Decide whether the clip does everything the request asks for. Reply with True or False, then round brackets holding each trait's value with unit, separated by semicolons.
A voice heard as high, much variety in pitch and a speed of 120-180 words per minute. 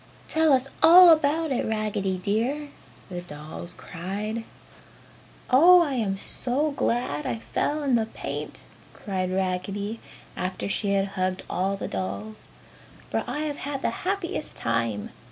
True (205 Hz; 7.6 semitones; 140 wpm)